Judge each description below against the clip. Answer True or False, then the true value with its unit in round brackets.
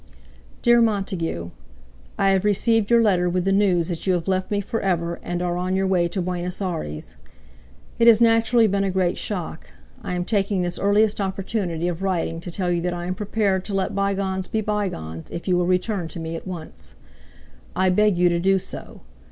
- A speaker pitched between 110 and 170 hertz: False (185 Hz)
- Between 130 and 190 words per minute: False (205 wpm)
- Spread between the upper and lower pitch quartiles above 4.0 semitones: False (2.5 semitones)